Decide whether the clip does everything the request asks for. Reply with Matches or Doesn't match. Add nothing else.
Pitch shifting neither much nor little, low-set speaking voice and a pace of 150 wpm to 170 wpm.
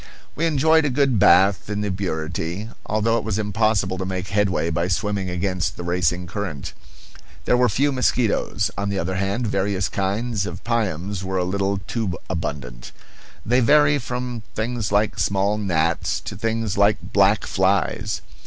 Matches